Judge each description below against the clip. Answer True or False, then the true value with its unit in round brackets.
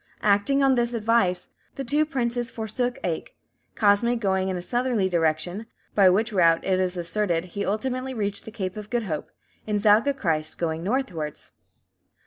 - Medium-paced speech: True (165 wpm)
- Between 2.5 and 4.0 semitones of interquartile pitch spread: False (4.8 semitones)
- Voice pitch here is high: True (205 Hz)